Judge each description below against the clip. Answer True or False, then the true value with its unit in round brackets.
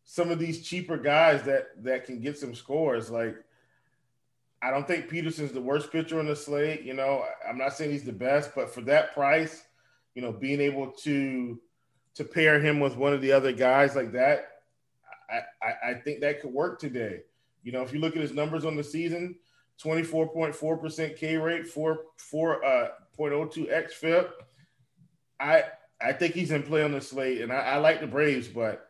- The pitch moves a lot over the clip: False (3.2 semitones)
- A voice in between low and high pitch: True (150 Hz)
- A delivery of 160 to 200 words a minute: True (195 wpm)